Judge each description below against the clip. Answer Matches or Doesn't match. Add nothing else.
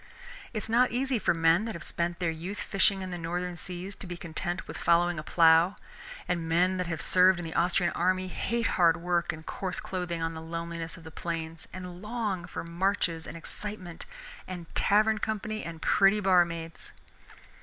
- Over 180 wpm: Matches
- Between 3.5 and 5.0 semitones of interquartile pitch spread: Doesn't match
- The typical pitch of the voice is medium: Matches